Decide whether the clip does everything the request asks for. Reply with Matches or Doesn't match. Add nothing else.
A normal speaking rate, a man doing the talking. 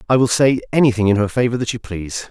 Doesn't match